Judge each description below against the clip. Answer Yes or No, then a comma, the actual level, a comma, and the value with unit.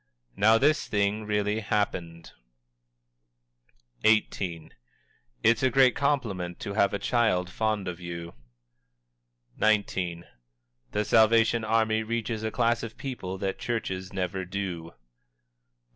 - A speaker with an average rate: No, slow, 115 wpm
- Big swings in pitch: No, average, 3.4 semitones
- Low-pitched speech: Yes, low, 105 Hz